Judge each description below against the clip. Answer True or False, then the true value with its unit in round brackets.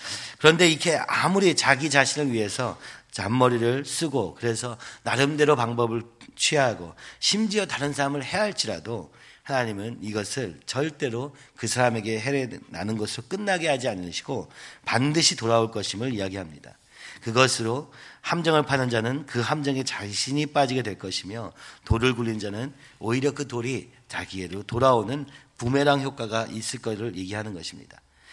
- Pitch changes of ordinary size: True (4.2 semitones)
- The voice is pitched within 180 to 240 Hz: False (125 Hz)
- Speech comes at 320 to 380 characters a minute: True (335 characters per minute)